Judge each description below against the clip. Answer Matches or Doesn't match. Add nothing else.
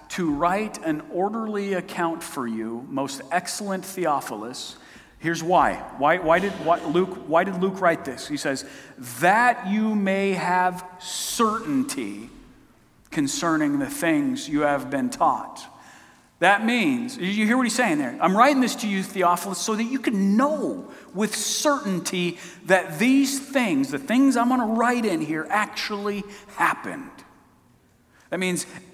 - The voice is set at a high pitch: Matches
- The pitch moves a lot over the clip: Matches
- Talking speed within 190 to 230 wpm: Doesn't match